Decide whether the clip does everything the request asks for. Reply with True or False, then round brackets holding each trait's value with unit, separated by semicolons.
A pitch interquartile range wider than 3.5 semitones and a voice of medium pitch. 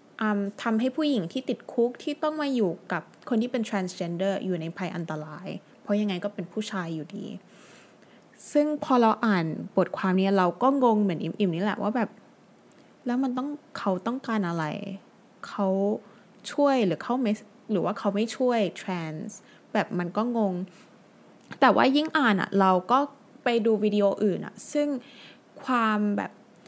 False (4.2 semitones; 210 Hz)